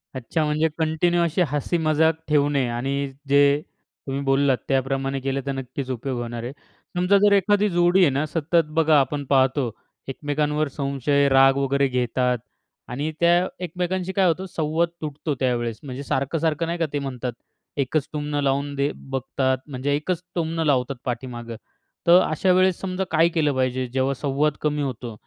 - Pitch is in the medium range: Yes, medium, 145 Hz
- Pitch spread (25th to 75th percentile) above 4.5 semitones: No, average, 3.3 semitones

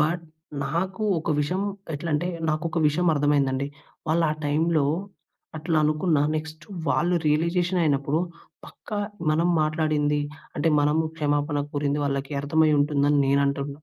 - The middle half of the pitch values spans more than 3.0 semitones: No, narrow, 2.4 semitones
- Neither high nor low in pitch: Yes, medium, 150 Hz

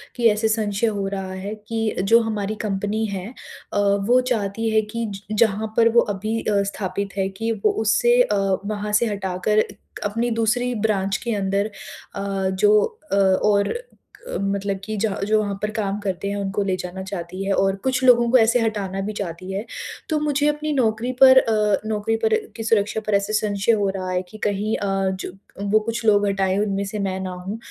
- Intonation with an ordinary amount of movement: No, narrow, 2.3 semitones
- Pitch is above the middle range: Yes, high, 205 Hz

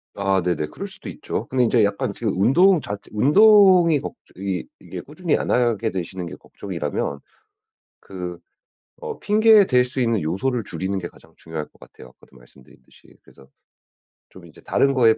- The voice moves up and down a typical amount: No, wide, 8.1 semitones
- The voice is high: No, low, 110 Hz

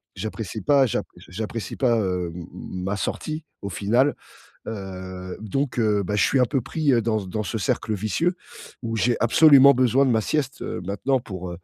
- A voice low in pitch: Yes, low, 110 Hz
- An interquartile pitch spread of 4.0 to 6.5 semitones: Yes, average, 5.1 semitones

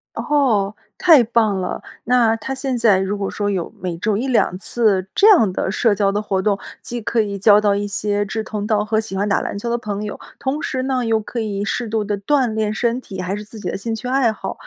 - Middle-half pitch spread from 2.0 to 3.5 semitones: Yes, average, 2.8 semitones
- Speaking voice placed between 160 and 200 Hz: No, high, 215 Hz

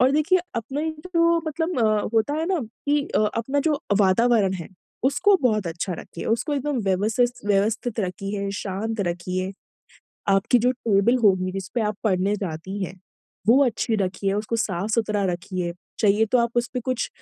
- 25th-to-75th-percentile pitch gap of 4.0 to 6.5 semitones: Yes, average, 4.3 semitones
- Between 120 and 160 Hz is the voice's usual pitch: No, high, 215 Hz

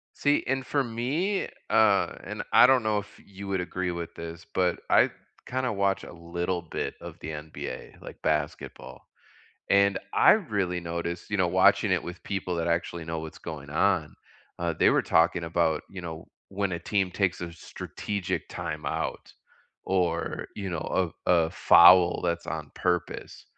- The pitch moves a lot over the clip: No, average, 2.9 semitones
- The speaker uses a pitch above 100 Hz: No, very low, 90 Hz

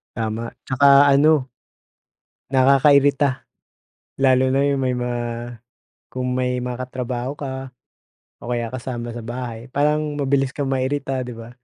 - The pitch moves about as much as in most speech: No, narrow, 2.0 semitones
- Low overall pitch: Yes, low, 130 Hz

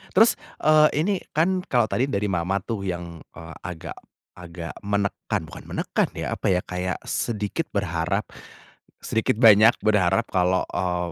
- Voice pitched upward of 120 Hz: No, low, 100 Hz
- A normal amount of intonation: Yes, average, 4.3 semitones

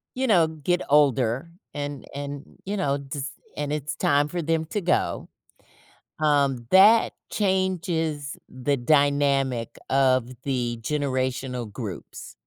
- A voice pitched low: No, medium, 145 Hz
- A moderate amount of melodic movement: Yes, average, 3.4 semitones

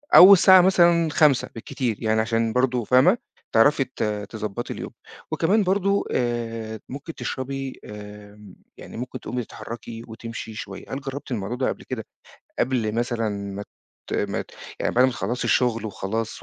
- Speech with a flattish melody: No, average, 3.6 semitones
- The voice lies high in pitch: No, low, 120 Hz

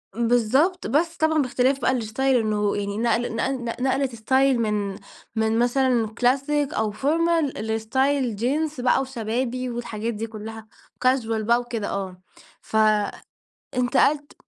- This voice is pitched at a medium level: No, high, 245 Hz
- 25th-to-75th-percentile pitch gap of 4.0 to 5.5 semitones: No, average, 3.4 semitones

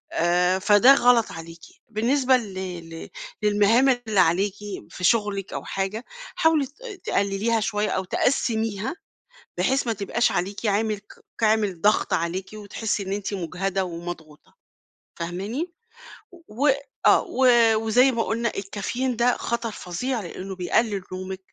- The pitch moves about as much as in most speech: Yes, average, 3.7 semitones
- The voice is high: Yes, high, 210 Hz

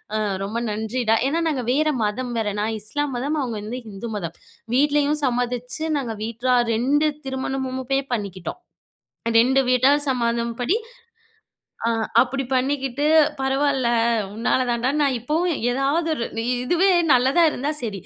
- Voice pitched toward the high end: Yes, very high, 255 Hz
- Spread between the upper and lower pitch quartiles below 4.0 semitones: Yes, average, 3.4 semitones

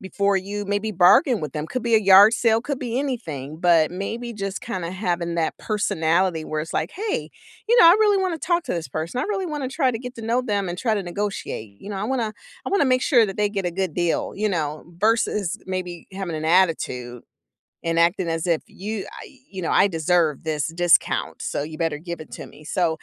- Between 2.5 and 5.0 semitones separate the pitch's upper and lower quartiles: No, wide, 5.4 semitones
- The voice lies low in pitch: No, high, 190 Hz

